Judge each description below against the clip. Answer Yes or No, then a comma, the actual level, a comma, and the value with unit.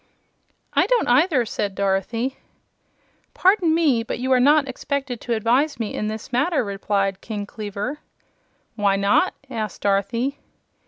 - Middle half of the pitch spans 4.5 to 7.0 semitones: Yes, wide, 5.4 semitones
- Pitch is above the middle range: Yes, high, 235 Hz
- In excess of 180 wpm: No, average, 140 wpm